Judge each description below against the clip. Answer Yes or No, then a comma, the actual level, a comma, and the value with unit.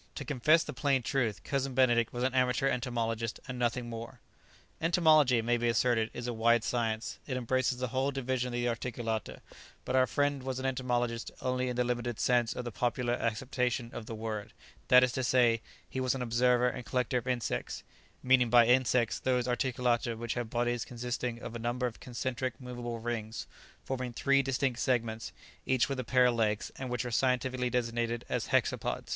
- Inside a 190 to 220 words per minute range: Yes, average, 195 wpm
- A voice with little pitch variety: Yes, narrow, 1.5 semitones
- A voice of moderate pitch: No, low, 125 Hz